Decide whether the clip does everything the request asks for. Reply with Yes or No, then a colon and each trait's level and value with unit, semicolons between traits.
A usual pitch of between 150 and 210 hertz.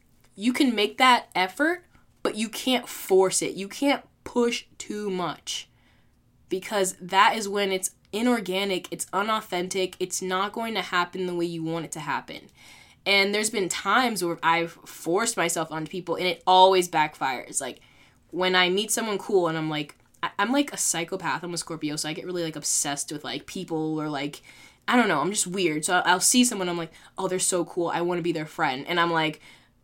Yes: medium, 185 Hz